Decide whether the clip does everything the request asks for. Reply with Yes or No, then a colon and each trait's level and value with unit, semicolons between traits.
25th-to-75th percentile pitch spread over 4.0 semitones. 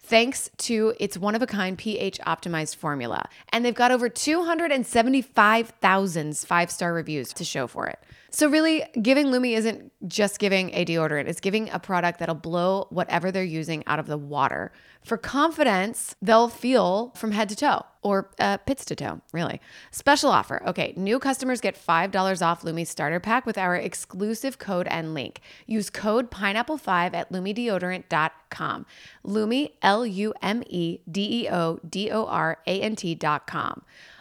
Yes: average, 5.2 semitones